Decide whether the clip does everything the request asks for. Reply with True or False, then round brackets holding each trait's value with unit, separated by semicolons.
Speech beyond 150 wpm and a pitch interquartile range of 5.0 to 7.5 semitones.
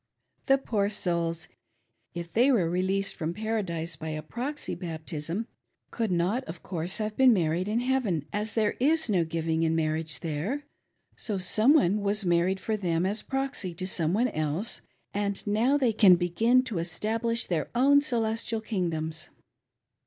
True (160 wpm; 5.3 semitones)